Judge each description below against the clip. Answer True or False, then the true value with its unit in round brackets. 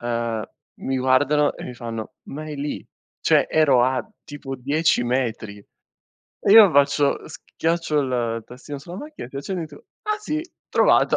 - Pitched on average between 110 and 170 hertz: True (140 Hz)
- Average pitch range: True (4.1 semitones)